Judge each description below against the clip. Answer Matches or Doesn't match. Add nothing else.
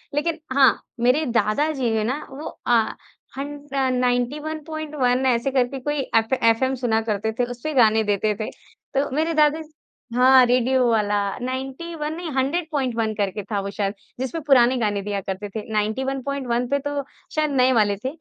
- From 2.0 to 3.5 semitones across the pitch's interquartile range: Doesn't match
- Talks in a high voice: Matches